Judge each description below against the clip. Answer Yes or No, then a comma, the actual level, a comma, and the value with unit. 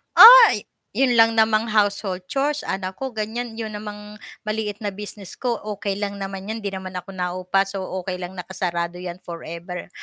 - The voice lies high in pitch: Yes, high, 200 Hz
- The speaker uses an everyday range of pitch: Yes, average, 3.1 semitones